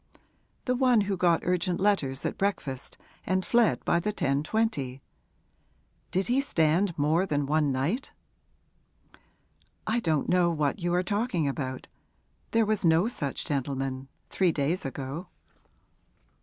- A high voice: No, medium, 170 Hz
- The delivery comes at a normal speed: No, slow, 130 wpm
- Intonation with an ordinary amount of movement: No, wide, 6.2 semitones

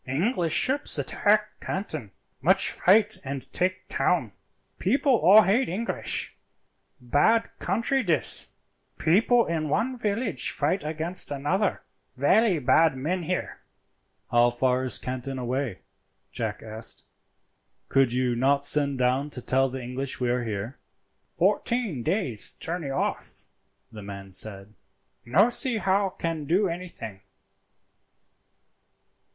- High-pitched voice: No, medium, 150 Hz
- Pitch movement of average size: No, wide, 7.4 semitones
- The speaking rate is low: Yes, slow, 120 wpm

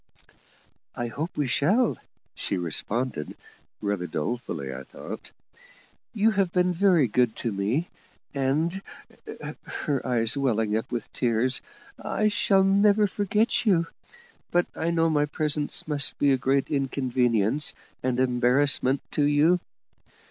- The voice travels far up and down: Yes, wide, 5.9 semitones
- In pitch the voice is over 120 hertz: Yes, medium, 140 Hz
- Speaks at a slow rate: Yes, slow, 125 wpm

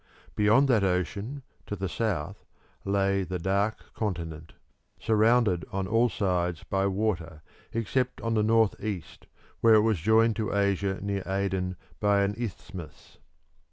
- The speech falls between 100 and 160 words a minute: Yes, average, 140 wpm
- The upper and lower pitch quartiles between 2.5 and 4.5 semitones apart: Yes, average, 3.1 semitones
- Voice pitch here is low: Yes, low, 100 Hz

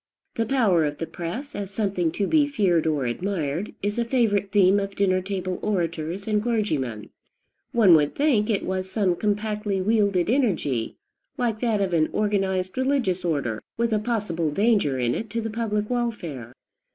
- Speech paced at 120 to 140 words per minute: No, average, 170 wpm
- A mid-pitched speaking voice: No, high, 200 Hz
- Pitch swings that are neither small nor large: Yes, average, 4.4 semitones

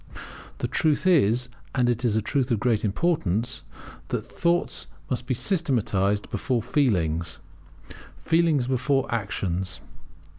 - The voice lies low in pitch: Yes, low, 120 Hz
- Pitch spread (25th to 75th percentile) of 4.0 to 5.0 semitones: No, wide, 5.5 semitones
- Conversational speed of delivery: No, slow, 120 wpm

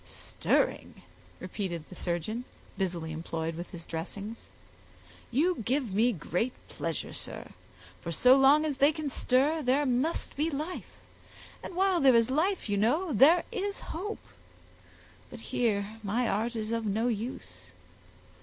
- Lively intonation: Yes, wide, 6.8 semitones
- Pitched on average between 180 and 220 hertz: No, high, 240 Hz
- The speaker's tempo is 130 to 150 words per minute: Yes, average, 145 wpm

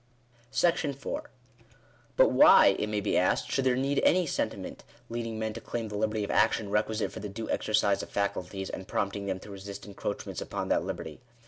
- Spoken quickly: No, average, 195 wpm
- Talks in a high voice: No, low, 110 Hz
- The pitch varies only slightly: No, average, 3.7 semitones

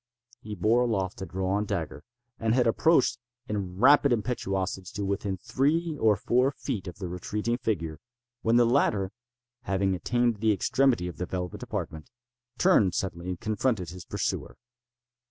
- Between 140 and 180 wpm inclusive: Yes, average, 155 wpm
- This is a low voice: Yes, low, 105 Hz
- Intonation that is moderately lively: Yes, average, 4.5 semitones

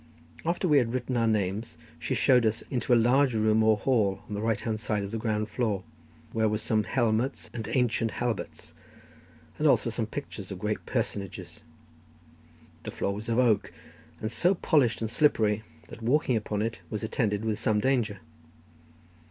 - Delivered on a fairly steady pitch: Yes, narrow, 2.3 semitones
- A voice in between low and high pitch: No, low, 110 Hz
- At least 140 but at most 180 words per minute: Yes, average, 175 wpm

